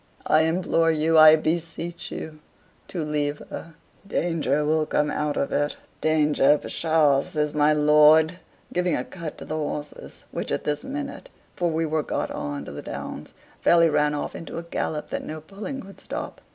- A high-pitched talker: No, medium, 155 Hz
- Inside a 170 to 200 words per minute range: Yes, average, 180 wpm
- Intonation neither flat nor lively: No, narrow, 1.9 semitones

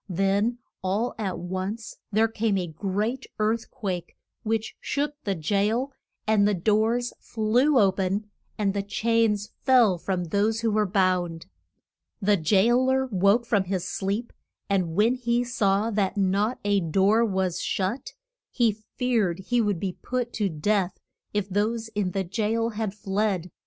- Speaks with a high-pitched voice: Yes, high, 205 Hz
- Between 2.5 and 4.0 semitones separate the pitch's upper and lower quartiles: Yes, average, 3.1 semitones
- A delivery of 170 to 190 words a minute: No, average, 155 wpm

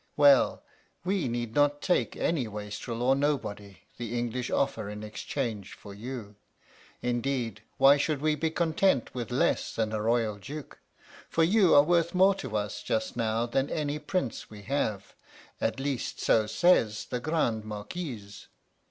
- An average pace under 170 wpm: Yes, average, 155 wpm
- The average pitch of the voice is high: No, low, 120 Hz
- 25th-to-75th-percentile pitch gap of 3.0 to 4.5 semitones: No, average, 5.2 semitones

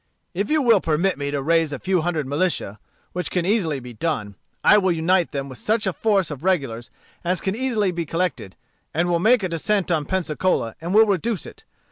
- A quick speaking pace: Yes, fast, 210 wpm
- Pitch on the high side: No, medium, 175 Hz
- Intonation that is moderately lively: Yes, average, 4.3 semitones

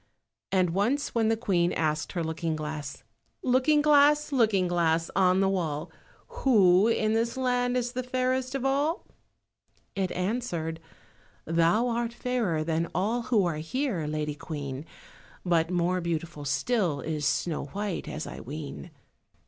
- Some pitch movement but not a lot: No, wide, 7.2 semitones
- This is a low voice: No, medium, 185 Hz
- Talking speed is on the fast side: No, average, 145 wpm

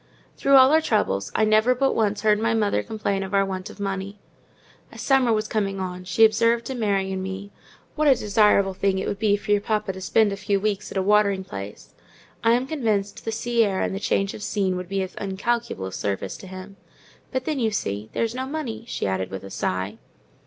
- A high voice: Yes, high, 205 Hz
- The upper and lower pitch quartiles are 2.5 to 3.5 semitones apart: Yes, average, 3.0 semitones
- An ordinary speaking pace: No, fast, 225 wpm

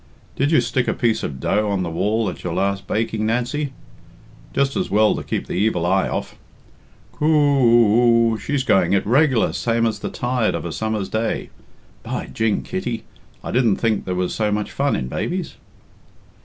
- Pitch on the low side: Yes, low, 115 Hz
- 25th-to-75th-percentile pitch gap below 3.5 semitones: No, average, 3.8 semitones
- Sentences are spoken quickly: No, average, 190 wpm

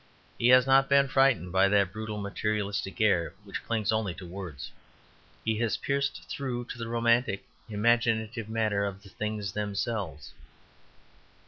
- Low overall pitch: Yes, low, 110 Hz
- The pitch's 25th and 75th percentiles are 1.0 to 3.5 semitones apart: Yes, average, 2.9 semitones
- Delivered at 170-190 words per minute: No, average, 145 wpm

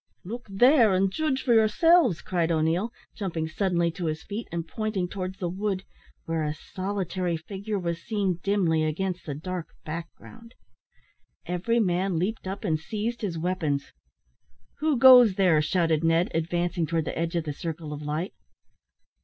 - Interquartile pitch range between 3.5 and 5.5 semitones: Yes, average, 3.9 semitones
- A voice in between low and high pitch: Yes, medium, 180 Hz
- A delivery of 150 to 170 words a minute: Yes, average, 160 wpm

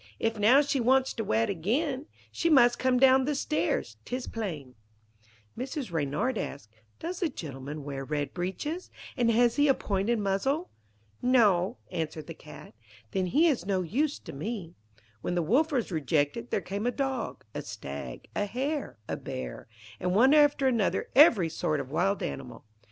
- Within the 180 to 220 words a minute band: No, average, 170 wpm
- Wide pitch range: Yes, wide, 8.6 semitones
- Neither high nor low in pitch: No, high, 215 Hz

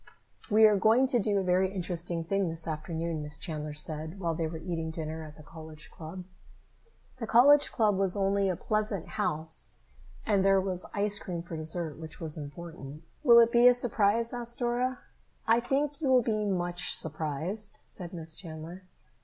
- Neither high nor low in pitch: Yes, medium, 180 Hz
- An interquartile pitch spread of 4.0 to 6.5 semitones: Yes, average, 5.0 semitones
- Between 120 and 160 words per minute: No, average, 180 wpm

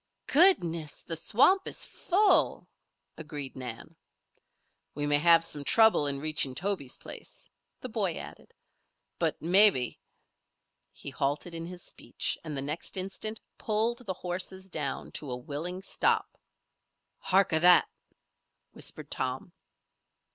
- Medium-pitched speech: Yes, medium, 170 Hz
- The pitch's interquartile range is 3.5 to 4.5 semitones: No, average, 5.0 semitones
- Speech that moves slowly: Yes, slow, 130 wpm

